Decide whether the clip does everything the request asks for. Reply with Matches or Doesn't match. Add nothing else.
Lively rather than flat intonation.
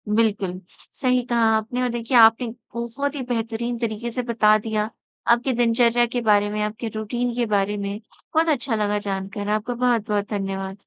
Doesn't match